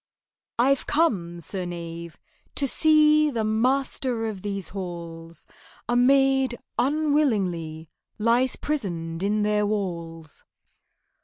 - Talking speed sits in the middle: No, slow, 100 wpm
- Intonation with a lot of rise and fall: Yes, wide, 7.7 semitones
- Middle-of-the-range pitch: No, high, 210 Hz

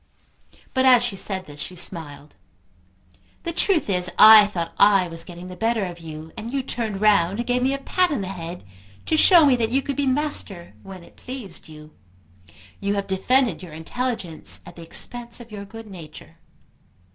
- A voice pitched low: No, high, 200 Hz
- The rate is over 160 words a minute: Yes, average, 190 wpm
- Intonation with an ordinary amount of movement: No, wide, 6.2 semitones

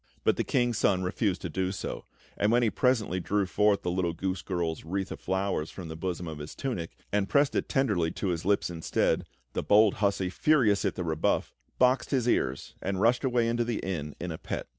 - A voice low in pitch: Yes, very low, 95 Hz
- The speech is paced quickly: Yes, fast, 220 wpm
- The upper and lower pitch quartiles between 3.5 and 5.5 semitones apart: Yes, average, 4.8 semitones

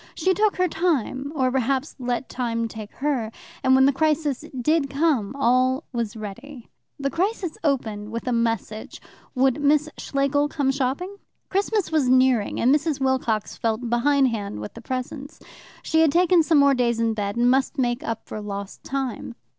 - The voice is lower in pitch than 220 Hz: No, very high, 265 Hz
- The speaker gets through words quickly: No, average, 175 wpm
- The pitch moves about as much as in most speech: Yes, average, 4.0 semitones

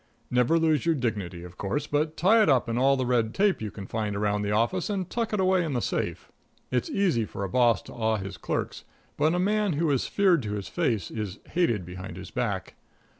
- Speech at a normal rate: No, fast, 230 wpm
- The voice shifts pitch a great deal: Yes, wide, 8.3 semitones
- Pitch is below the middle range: Yes, low, 125 Hz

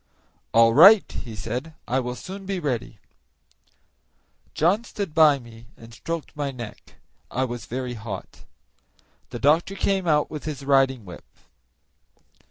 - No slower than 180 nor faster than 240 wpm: No, average, 140 wpm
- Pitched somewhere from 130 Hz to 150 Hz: Yes, low, 135 Hz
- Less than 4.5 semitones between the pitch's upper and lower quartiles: No, wide, 5.6 semitones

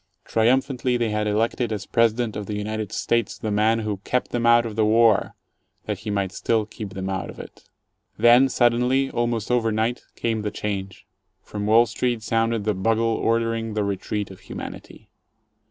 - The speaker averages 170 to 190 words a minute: Yes, average, 180 wpm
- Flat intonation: Yes, narrow, 2.0 semitones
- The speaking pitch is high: No, low, 110 Hz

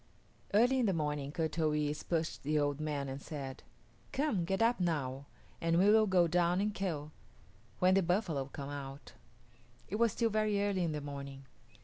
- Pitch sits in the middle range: Yes, medium, 165 Hz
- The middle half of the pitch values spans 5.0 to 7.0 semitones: Yes, average, 5.3 semitones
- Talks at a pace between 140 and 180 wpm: No, average, 190 wpm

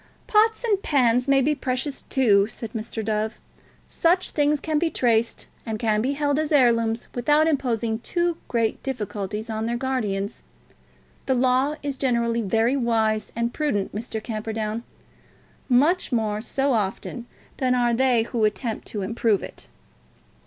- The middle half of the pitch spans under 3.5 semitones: No, average, 3.8 semitones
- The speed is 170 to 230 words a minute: No, average, 150 wpm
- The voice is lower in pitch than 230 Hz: No, high, 235 Hz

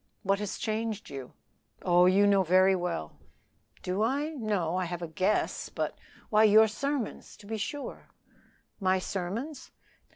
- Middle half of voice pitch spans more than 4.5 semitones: No, average, 3.3 semitones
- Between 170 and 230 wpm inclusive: No, average, 155 wpm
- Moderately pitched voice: No, high, 200 Hz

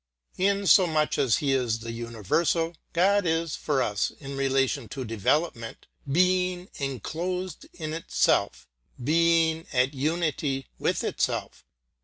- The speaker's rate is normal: No, slow, 125 wpm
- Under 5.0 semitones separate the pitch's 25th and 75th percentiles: Yes, average, 4.5 semitones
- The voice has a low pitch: No, medium, 155 Hz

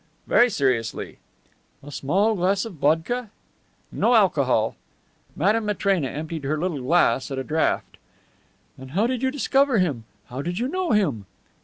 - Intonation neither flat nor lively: No, wide, 7.9 semitones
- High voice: No, medium, 175 Hz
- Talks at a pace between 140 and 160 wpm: Yes, average, 150 wpm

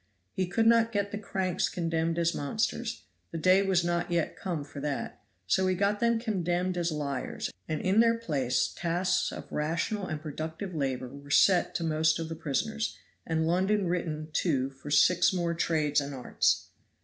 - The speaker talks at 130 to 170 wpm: No, average, 180 wpm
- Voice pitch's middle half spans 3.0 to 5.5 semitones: Yes, average, 3.7 semitones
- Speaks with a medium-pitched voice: Yes, medium, 170 Hz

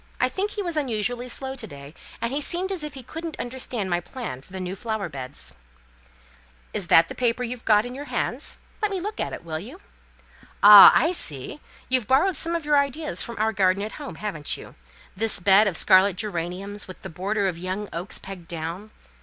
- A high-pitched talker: Yes, high, 215 Hz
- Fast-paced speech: Yes, fast, 210 wpm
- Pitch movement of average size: No, wide, 6.6 semitones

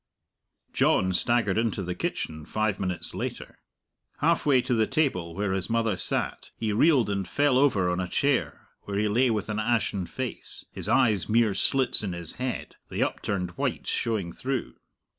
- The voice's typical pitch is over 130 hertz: No, low, 110 Hz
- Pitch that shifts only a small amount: No, average, 4.9 semitones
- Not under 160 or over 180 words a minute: Yes, average, 170 wpm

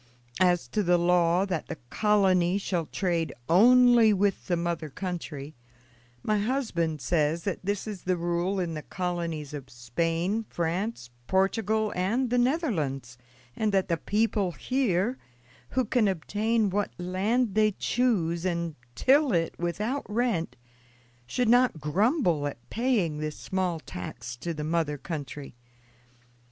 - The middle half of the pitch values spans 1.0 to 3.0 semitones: No, average, 4.7 semitones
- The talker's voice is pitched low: No, medium, 180 Hz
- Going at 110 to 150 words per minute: Yes, average, 140 wpm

